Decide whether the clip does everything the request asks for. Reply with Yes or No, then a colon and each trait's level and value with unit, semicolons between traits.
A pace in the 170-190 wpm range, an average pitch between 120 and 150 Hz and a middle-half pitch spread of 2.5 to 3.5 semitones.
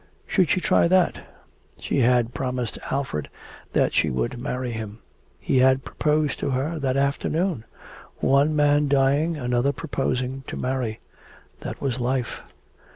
No: average, 140 wpm; low, 135 Hz; average, 2.8 semitones